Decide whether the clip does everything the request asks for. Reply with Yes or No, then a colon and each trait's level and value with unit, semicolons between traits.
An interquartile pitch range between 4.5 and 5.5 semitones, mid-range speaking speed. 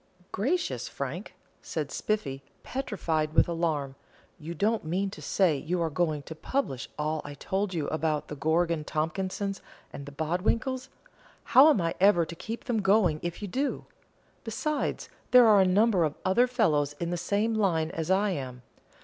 Yes: average, 5.2 semitones; average, 170 wpm